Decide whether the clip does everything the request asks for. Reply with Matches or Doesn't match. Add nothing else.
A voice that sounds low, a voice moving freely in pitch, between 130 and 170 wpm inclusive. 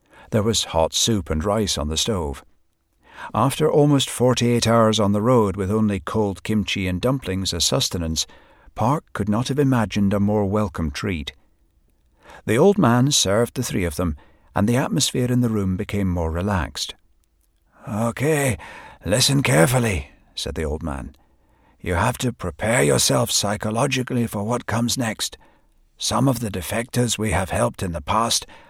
Matches